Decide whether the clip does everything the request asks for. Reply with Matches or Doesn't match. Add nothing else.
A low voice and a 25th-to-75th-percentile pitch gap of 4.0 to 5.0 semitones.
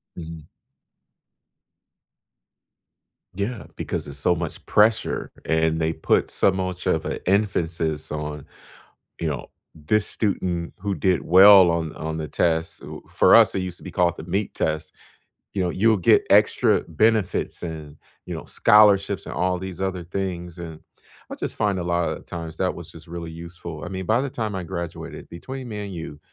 Doesn't match